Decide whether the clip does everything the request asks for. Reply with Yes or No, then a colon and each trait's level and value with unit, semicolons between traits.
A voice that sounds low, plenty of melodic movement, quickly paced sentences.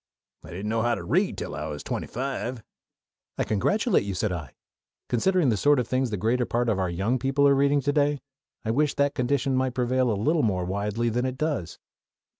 No: low, 125 Hz; average, 4.8 semitones; fast, 220 wpm